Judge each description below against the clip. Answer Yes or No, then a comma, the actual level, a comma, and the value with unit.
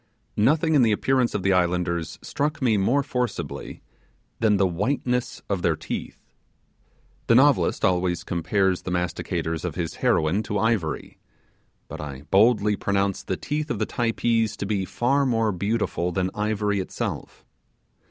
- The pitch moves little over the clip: No, average, 4.8 semitones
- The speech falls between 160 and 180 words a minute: No, average, 150 wpm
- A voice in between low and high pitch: No, low, 105 Hz